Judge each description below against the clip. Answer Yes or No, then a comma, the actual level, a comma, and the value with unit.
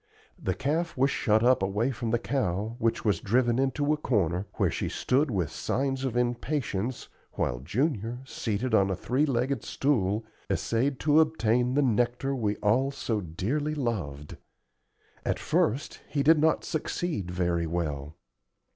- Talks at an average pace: Yes, average, 155 wpm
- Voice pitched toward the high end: No, low, 120 Hz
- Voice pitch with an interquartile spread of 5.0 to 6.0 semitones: Yes, wide, 5.5 semitones